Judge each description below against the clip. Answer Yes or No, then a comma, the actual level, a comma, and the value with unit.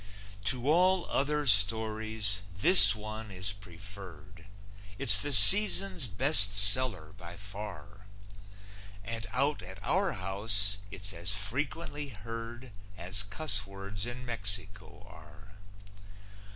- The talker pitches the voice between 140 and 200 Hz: No, low, 105 Hz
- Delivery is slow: Yes, slow, 110 wpm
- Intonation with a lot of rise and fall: No, average, 3.1 semitones